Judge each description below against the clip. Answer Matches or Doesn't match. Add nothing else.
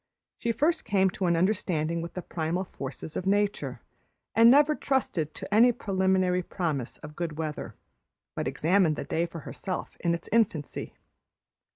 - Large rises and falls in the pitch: Doesn't match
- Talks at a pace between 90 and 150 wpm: Doesn't match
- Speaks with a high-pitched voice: Doesn't match